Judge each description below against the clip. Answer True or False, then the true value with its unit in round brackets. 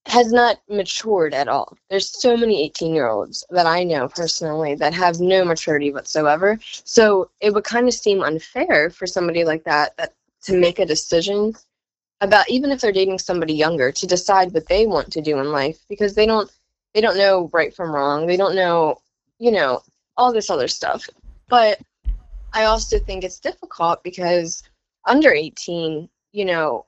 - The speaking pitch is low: False (185 Hz)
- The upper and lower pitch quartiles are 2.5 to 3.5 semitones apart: False (4.7 semitones)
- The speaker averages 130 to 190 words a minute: True (180 wpm)